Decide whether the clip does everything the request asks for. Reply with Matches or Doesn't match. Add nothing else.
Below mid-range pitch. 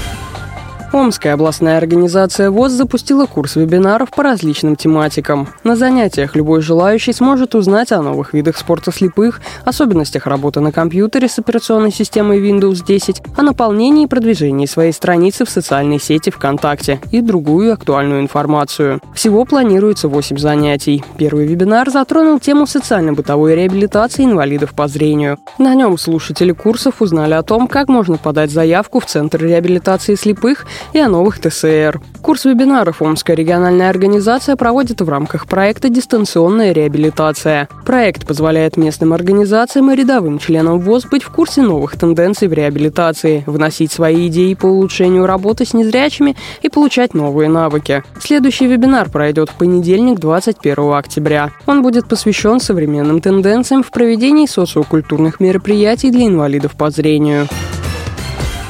Doesn't match